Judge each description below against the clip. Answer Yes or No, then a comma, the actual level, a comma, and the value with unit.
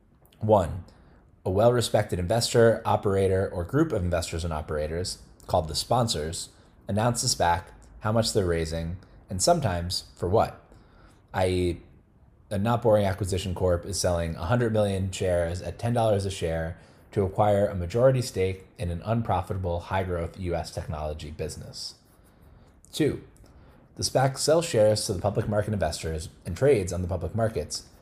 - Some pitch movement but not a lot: Yes, average, 3.9 semitones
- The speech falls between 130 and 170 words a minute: Yes, average, 150 wpm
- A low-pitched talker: Yes, very low, 95 Hz